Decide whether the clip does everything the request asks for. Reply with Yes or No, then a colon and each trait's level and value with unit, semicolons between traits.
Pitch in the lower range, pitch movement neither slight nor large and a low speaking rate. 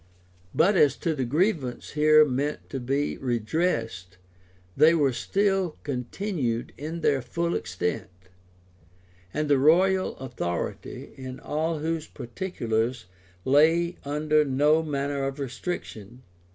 No: medium, 145 Hz; average, 4.4 semitones; slow, 115 wpm